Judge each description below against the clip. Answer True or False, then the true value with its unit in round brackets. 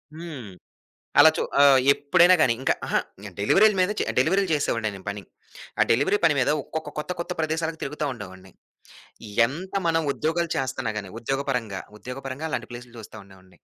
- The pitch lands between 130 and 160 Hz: True (140 Hz)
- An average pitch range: False (6.0 semitones)